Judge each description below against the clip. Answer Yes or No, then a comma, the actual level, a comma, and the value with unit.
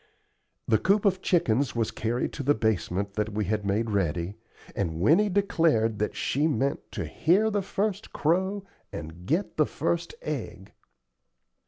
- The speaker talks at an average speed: Yes, average, 155 wpm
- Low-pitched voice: Yes, low, 125 Hz